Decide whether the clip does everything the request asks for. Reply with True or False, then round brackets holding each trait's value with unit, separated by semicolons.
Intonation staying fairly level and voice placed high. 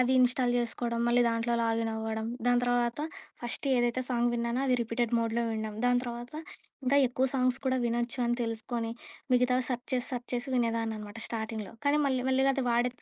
True (1.5 semitones; 240 Hz)